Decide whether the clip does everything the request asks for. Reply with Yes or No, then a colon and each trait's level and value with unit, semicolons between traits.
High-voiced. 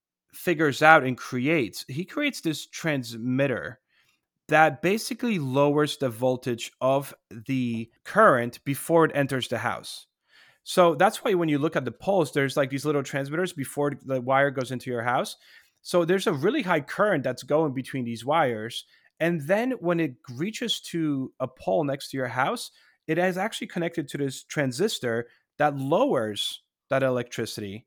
No: medium, 140 Hz